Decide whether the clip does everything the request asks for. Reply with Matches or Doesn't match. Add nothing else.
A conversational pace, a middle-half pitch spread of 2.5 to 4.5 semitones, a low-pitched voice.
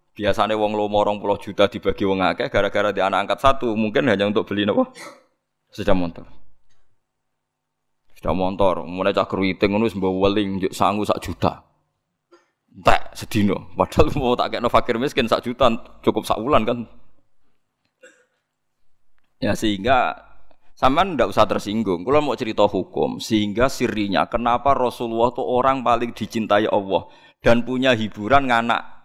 Doesn't match